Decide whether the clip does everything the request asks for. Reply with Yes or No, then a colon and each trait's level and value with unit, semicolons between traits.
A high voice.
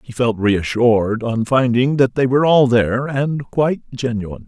No: low, 125 Hz